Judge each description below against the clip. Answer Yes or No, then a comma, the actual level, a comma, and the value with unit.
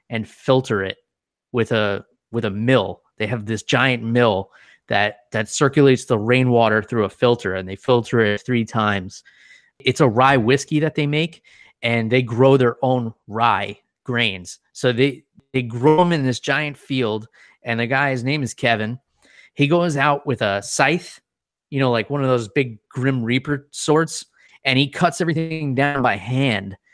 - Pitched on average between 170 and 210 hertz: No, low, 125 Hz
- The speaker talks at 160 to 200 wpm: Yes, average, 180 wpm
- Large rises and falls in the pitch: No, average, 3.7 semitones